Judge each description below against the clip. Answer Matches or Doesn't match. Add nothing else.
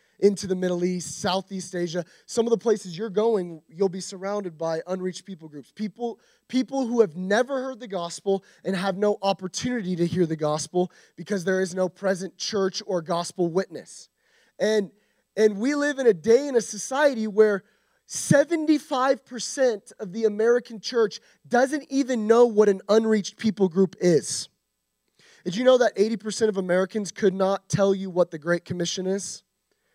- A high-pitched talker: Matches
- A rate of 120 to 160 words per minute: Doesn't match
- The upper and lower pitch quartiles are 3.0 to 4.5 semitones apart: Matches